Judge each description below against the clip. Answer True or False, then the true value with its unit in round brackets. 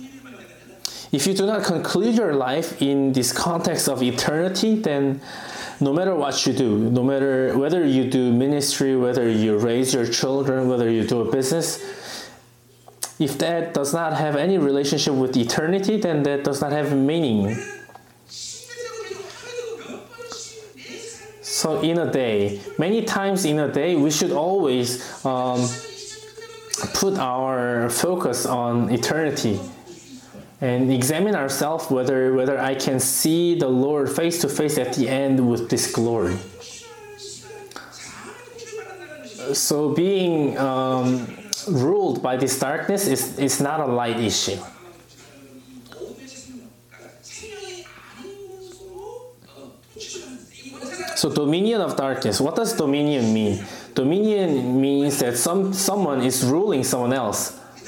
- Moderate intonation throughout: False (8.2 semitones)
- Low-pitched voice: False (145 Hz)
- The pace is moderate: False (120 wpm)